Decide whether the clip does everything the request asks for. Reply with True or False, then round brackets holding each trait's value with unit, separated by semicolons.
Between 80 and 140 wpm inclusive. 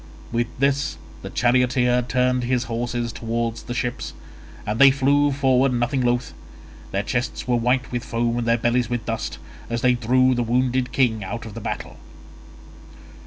False (165 wpm)